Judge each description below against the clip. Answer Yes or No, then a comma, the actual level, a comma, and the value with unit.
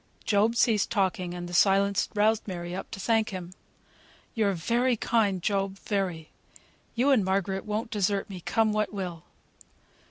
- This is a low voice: No, high, 200 Hz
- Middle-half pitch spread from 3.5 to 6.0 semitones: No, average, 2.8 semitones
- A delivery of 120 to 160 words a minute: Yes, average, 155 wpm